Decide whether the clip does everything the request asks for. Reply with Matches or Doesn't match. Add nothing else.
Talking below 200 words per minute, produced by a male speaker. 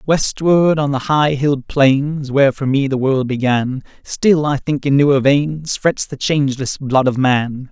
Matches